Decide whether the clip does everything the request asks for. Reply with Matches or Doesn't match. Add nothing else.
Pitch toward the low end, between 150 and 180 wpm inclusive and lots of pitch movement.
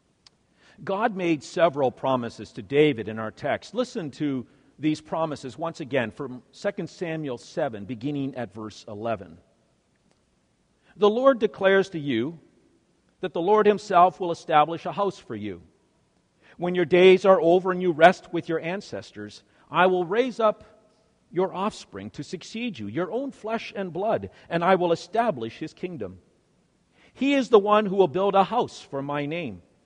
Doesn't match